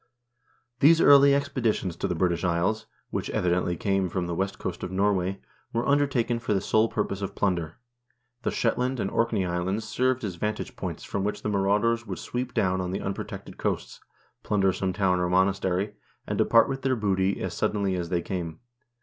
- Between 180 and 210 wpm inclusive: Yes, average, 190 wpm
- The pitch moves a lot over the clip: No, average, 3.9 semitones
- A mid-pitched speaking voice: No, low, 100 Hz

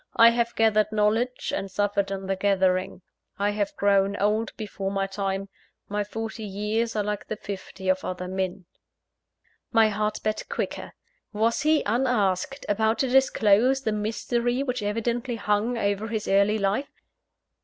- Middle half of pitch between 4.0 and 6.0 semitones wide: No, narrow, 2.4 semitones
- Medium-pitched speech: No, high, 210 Hz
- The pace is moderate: Yes, average, 155 wpm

